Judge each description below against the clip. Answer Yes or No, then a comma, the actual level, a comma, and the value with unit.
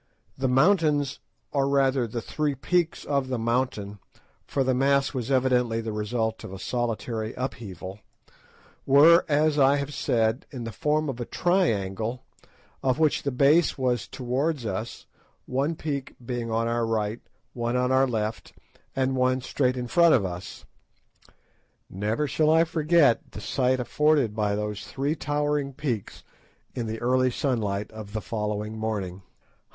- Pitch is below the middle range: Yes, low, 125 Hz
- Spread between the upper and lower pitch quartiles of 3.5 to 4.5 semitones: Yes, average, 4.1 semitones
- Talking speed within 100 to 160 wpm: Yes, average, 155 wpm